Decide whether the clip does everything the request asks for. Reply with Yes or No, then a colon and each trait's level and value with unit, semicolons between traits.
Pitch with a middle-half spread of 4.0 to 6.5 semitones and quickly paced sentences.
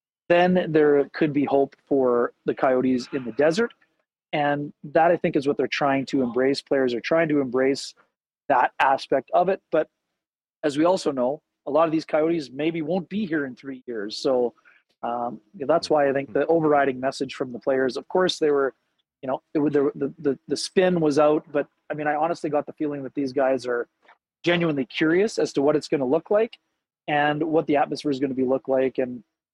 No: average, 3.1 semitones; fast, 215 wpm